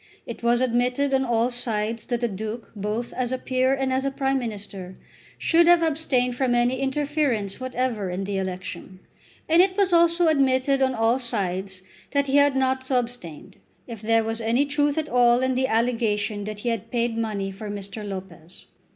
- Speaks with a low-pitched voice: No, high, 240 Hz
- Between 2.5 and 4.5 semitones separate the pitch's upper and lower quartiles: Yes, average, 4.0 semitones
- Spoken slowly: No, average, 190 wpm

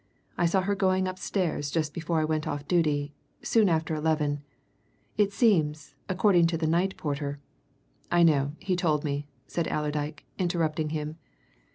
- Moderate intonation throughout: Yes, average, 3.1 semitones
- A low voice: No, medium, 160 Hz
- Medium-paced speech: Yes, average, 160 wpm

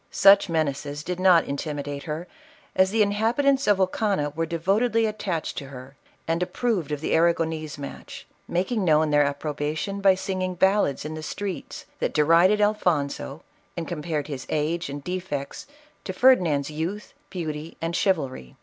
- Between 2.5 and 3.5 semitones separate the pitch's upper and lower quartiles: No, average, 4.6 semitones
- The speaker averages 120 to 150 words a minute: No, average, 160 wpm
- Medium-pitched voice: Yes, medium, 165 Hz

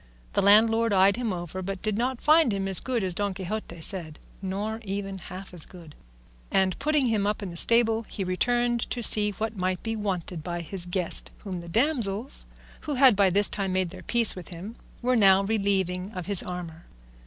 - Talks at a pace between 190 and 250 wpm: Yes, average, 200 wpm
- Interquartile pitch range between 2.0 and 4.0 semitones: Yes, average, 3.5 semitones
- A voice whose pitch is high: Yes, high, 195 Hz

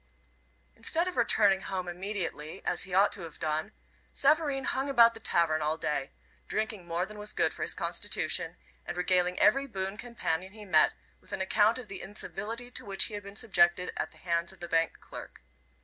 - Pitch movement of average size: Yes, average, 4.4 semitones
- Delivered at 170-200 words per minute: Yes, average, 195 wpm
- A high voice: Yes, high, 195 Hz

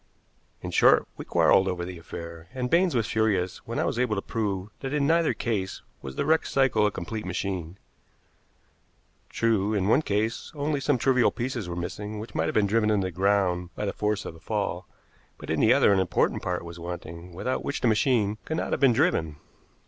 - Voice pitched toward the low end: Yes, low, 105 Hz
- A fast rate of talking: Yes, fast, 210 wpm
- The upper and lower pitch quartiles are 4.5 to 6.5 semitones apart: Yes, average, 5.3 semitones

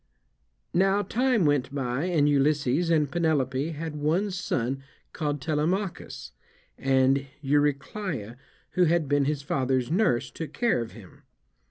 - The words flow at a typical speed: No, slow, 130 wpm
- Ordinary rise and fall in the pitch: Yes, average, 4.2 semitones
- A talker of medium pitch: Yes, medium, 145 Hz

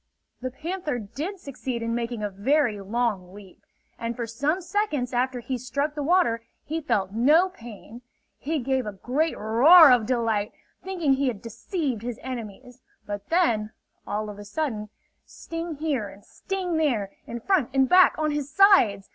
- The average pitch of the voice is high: Yes, very high, 255 Hz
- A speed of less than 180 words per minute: Yes, average, 170 wpm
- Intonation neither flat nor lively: No, wide, 5.9 semitones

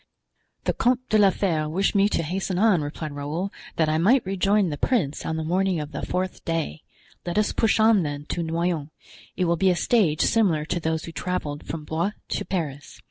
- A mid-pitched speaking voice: Yes, medium, 170 Hz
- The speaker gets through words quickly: Yes, fast, 210 wpm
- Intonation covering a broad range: No, average, 4.0 semitones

